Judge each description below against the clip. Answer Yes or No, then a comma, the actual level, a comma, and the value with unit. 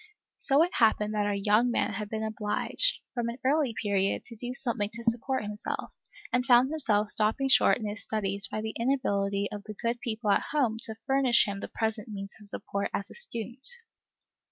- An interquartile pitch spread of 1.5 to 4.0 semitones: Yes, average, 3.0 semitones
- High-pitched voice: Yes, high, 220 Hz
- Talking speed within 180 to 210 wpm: Yes, average, 200 wpm